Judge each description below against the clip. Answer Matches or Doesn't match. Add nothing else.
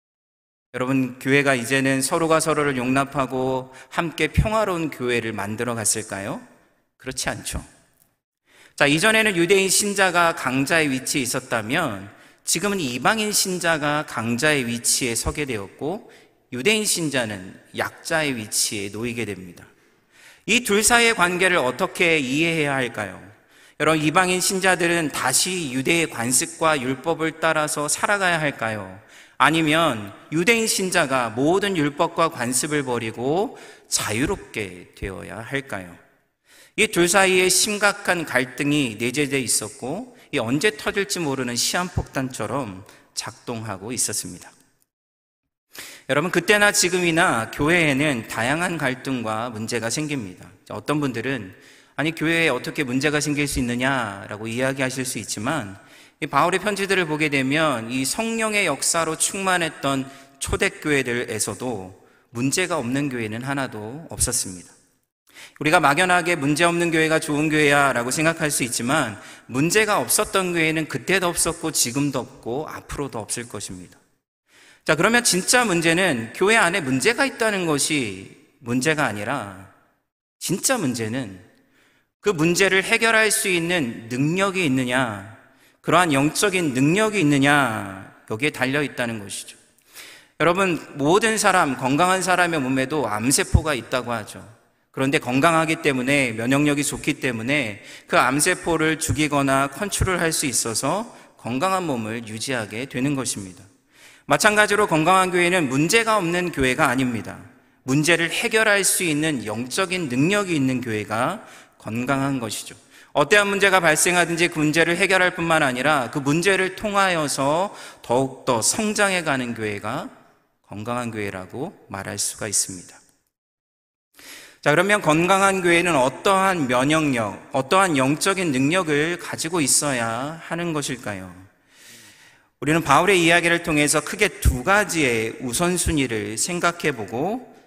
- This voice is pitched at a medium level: Matches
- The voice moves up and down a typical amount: Doesn't match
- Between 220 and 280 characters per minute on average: Doesn't match